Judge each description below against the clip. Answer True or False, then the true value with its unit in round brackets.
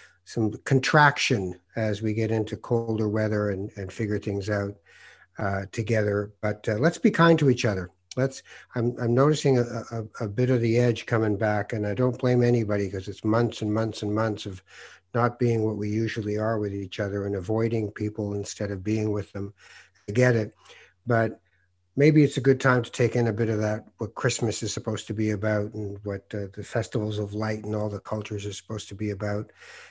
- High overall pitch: False (110 Hz)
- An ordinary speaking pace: False (210 wpm)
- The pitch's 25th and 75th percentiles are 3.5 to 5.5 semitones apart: False (2.4 semitones)